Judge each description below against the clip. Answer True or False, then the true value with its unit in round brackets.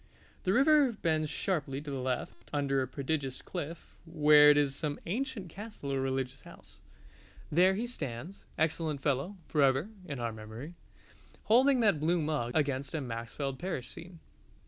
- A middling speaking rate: True (150 wpm)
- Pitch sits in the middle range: True (150 Hz)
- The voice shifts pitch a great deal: False (4.8 semitones)